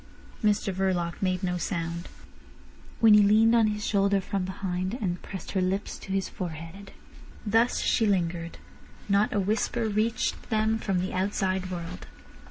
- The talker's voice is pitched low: No, high, 195 Hz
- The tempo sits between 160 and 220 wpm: No, average, 150 wpm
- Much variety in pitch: No, narrow, 2.5 semitones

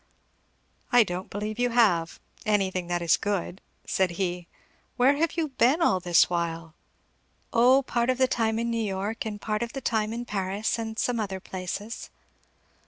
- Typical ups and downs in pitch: Yes, average, 4.2 semitones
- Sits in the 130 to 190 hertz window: No, high, 215 Hz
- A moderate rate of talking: Yes, average, 170 wpm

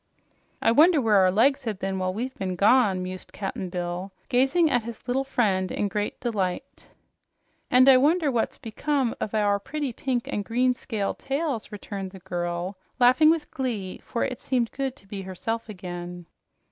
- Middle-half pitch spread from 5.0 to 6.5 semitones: Yes, wide, 5.4 semitones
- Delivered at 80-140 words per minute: No, average, 175 wpm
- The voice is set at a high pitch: Yes, high, 225 Hz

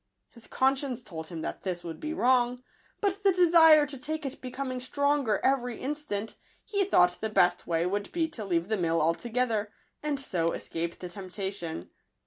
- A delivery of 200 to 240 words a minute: No, average, 180 wpm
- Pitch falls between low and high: No, high, 240 Hz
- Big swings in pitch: Yes, wide, 7.9 semitones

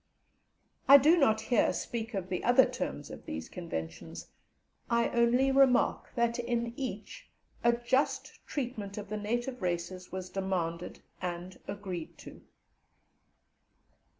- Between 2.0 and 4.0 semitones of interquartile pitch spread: No, average, 4.9 semitones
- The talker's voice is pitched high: Yes, high, 220 Hz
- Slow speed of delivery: Yes, slow, 125 wpm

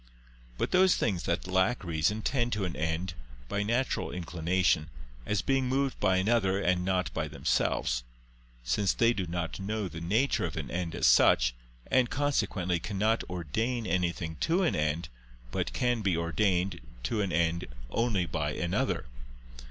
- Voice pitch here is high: No, very low, 95 Hz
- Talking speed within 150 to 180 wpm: Yes, average, 160 wpm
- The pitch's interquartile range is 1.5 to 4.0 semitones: No, average, 4.9 semitones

